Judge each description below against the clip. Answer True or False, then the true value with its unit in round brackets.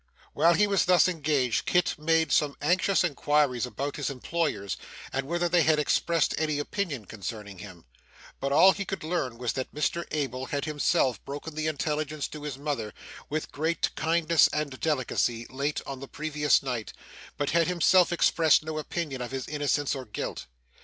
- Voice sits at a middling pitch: True (150 Hz)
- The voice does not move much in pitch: False (3.5 semitones)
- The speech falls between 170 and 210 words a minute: True (175 wpm)